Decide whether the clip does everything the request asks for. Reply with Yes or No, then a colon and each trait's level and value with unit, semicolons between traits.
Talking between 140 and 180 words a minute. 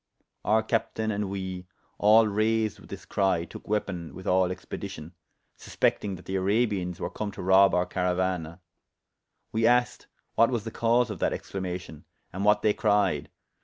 Yes: average, 165 wpm